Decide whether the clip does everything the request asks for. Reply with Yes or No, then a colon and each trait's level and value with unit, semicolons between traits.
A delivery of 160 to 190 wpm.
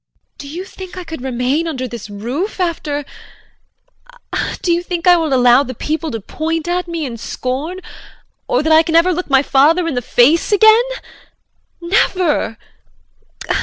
Yes: average, 165 wpm